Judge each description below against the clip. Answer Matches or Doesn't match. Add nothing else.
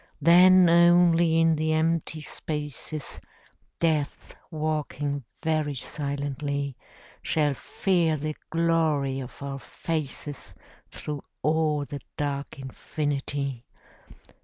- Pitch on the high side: Doesn't match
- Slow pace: Matches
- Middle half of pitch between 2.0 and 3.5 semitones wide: Matches